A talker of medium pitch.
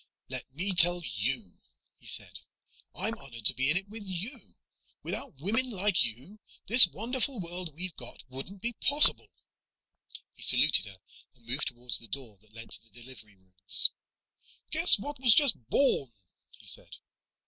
Yes: medium, 155 Hz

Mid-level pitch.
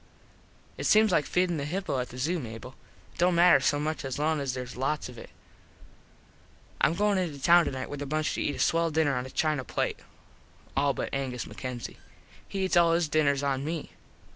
Yes: medium, 150 Hz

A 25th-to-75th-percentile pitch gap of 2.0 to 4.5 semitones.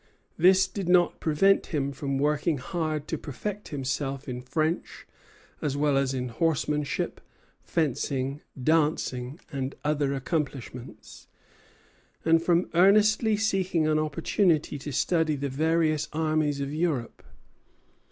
Yes: average, 3.3 semitones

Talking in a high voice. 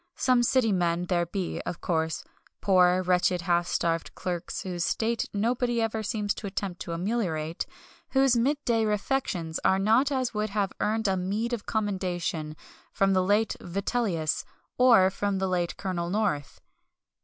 Yes: high, 195 Hz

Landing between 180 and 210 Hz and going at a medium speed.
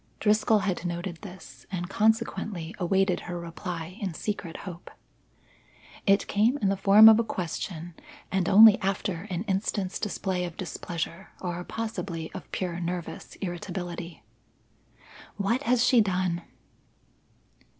No: high, 190 Hz; slow, 130 wpm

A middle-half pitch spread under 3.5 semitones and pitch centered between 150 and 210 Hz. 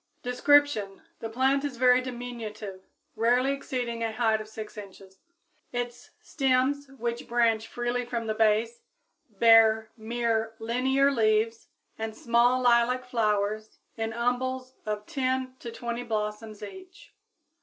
No: narrow, 2.5 semitones; high, 235 Hz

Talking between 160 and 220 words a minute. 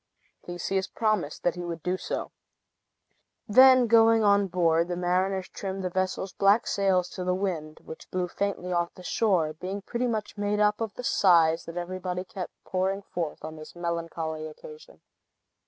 Yes: average, 170 wpm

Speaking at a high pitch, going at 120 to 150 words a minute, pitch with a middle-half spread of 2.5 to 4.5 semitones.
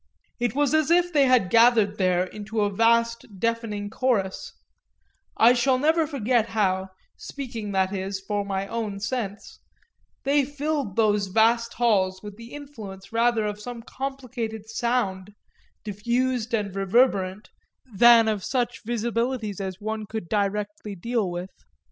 Yes: high, 220 Hz; average, 140 wpm; average, 3.3 semitones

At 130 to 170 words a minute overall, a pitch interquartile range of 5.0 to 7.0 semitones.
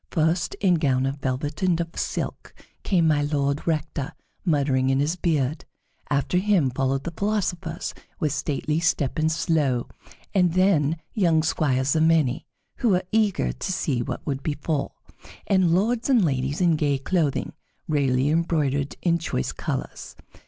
No: average, 150 wpm; average, 3.8 semitones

